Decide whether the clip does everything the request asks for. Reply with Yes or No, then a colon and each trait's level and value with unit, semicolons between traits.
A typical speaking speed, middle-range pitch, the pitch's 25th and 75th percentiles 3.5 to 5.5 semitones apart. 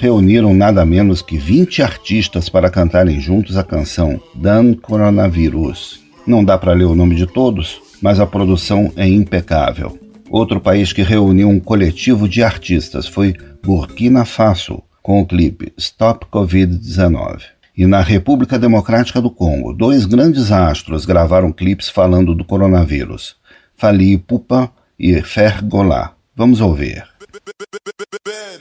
No: average, 130 wpm; low, 100 Hz; average, 4.0 semitones